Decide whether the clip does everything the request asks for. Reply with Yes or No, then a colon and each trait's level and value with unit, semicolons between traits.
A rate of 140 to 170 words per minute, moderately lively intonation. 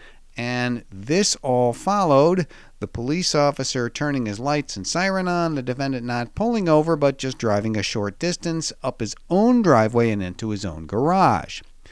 No: average, 165 wpm; wide, 6.2 semitones